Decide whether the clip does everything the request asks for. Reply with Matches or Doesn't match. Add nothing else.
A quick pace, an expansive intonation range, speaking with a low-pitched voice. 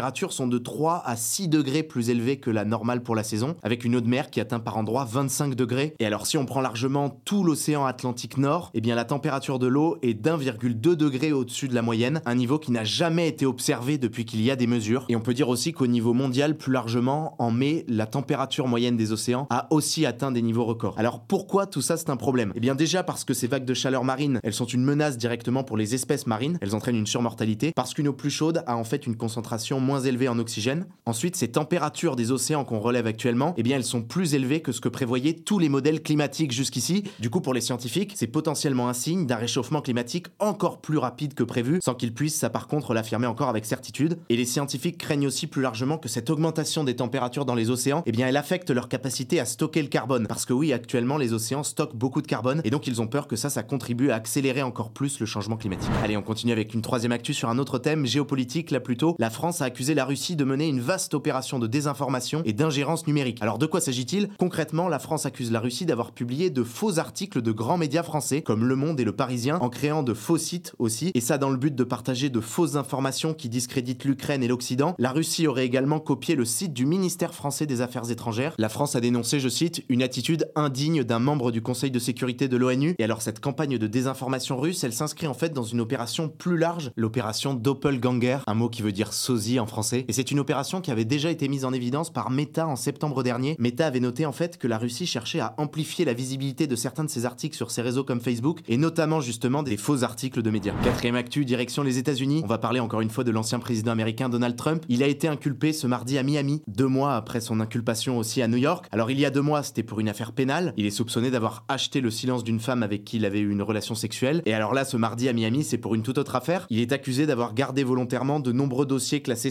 Doesn't match